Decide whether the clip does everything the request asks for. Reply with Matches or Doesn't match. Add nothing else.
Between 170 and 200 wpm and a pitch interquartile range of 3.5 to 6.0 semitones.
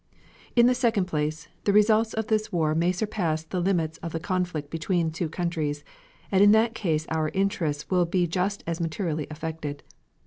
Matches